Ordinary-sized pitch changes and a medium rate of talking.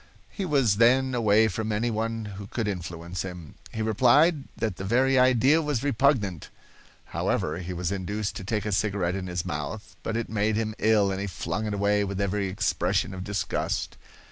Yes: average, 3.4 semitones; average, 190 wpm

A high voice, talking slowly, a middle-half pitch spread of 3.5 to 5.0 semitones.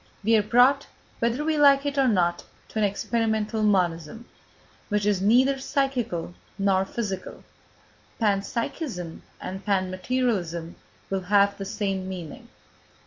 Yes: high, 210 Hz; slow, 125 wpm; average, 4.3 semitones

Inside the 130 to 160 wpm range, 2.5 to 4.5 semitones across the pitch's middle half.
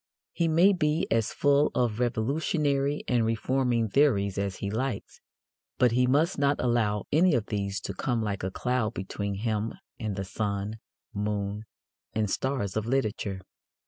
No: average, 155 wpm; average, 4.9 semitones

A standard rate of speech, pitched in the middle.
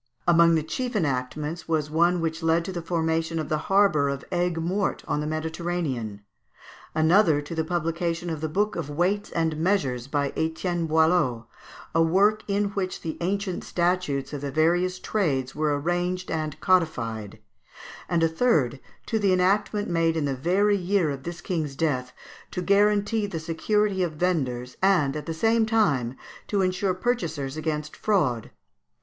Yes: average, 165 wpm; medium, 165 Hz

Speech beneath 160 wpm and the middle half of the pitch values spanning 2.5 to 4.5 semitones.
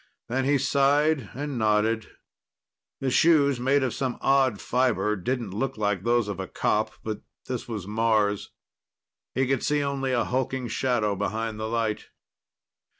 Yes: average, 150 wpm; average, 3.9 semitones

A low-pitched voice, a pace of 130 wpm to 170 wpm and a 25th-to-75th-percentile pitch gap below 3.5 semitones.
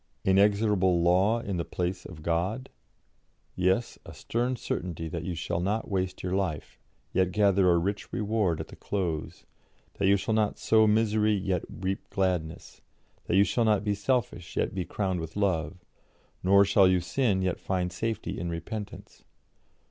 Yes: very low, 95 Hz; average, 165 wpm; average, 2.8 semitones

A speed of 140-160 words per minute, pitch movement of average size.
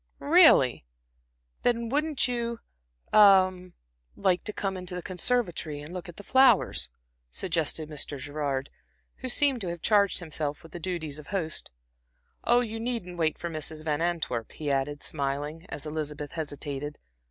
No: average, 155 wpm; wide, 5.7 semitones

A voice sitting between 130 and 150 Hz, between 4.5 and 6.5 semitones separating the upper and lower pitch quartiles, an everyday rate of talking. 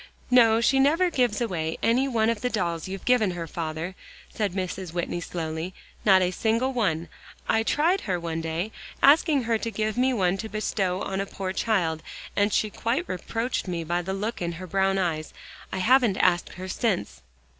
No: high, 195 Hz; average, 4.8 semitones; average, 190 wpm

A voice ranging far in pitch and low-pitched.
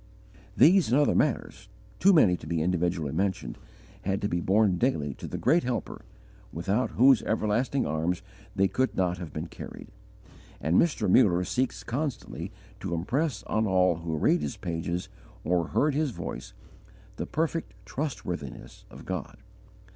Yes: wide, 7.3 semitones; very low, 95 Hz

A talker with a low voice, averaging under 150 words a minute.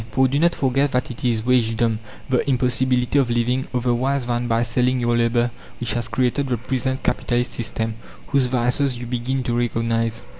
No: low, 125 Hz; average, 180 wpm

